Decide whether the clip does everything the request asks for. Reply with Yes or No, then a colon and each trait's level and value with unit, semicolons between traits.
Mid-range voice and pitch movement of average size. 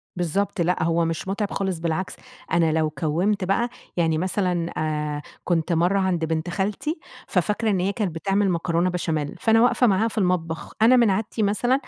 Yes: medium, 180 Hz; average, 3.7 semitones